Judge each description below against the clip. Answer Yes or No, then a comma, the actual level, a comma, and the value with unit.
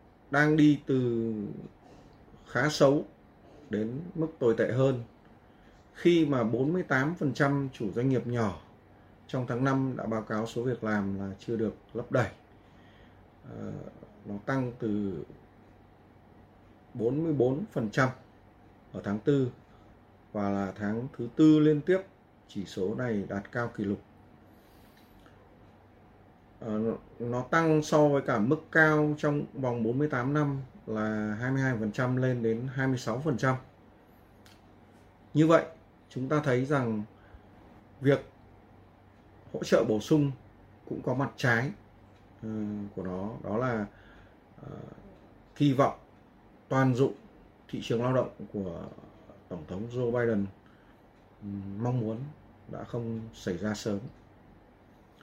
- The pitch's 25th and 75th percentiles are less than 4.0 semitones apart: No, average, 4.3 semitones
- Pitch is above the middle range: No, low, 115 Hz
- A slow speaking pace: Yes, slow, 115 wpm